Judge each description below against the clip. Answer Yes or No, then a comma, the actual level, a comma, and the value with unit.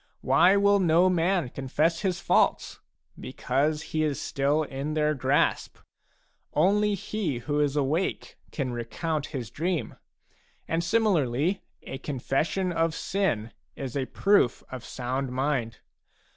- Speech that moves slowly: Yes, slow, 130 wpm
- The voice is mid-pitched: Yes, medium, 150 Hz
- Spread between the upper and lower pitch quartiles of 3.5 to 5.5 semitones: Yes, average, 5.0 semitones